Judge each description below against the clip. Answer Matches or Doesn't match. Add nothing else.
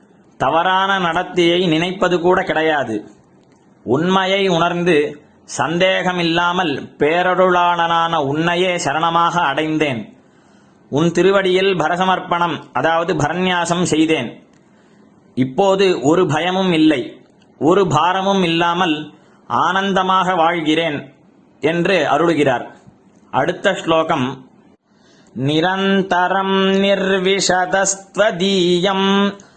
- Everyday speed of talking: Doesn't match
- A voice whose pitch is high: Doesn't match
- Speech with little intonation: Matches